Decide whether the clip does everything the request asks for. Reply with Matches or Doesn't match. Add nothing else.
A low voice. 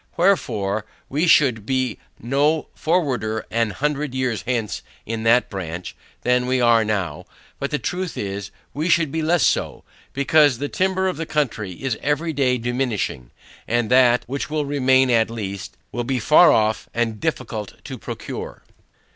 Matches